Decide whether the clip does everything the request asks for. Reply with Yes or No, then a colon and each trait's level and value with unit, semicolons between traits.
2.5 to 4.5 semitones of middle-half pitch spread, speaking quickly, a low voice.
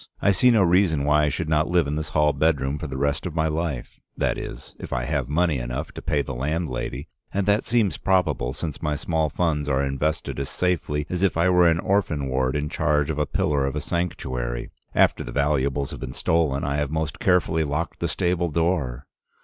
Yes: average, 3.4 semitones; fast, 220 wpm; very low, 75 Hz